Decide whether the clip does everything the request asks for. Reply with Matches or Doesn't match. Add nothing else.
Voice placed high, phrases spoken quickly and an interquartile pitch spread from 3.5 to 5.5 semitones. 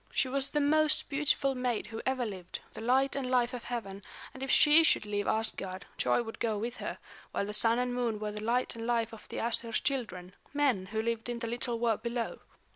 Doesn't match